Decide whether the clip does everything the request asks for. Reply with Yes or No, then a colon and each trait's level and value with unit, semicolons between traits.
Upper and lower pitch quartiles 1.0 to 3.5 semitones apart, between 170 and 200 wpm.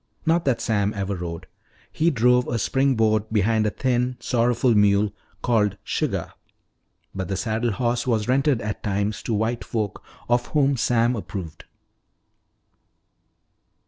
No: average, 3.1 semitones; average, 140 wpm